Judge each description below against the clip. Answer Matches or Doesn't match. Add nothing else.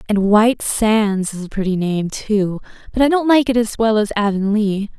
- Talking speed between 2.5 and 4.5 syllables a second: Doesn't match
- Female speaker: Matches